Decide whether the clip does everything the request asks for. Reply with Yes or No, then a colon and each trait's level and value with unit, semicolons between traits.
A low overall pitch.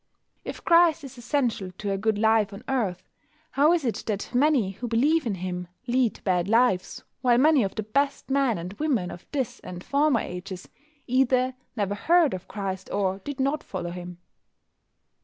No: high, 230 Hz